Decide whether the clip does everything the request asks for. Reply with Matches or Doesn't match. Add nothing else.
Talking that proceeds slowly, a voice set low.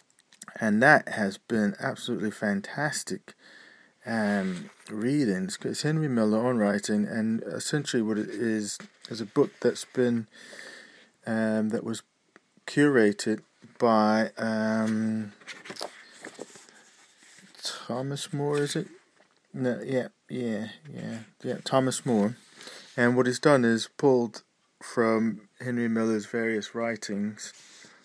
Matches